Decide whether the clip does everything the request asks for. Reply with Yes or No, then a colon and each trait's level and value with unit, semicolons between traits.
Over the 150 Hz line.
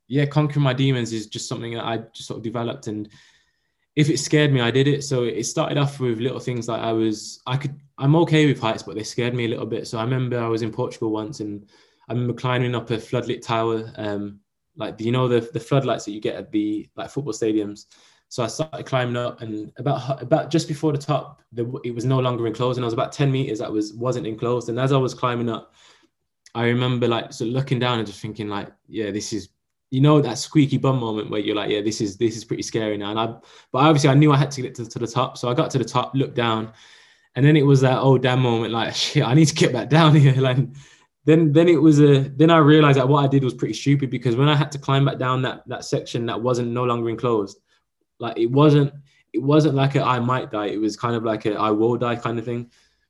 No: low, 125 Hz